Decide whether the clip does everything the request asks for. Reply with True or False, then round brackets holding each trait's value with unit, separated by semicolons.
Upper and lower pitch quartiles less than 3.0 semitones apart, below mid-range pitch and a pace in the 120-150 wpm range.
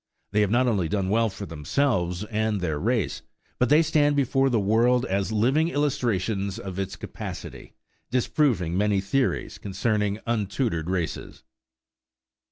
False (4.6 semitones; 105 Hz; 140 wpm)